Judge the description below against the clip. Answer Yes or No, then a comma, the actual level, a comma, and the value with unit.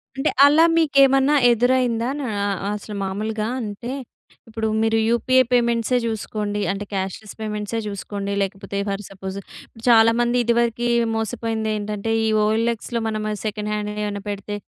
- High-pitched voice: Yes, high, 220 Hz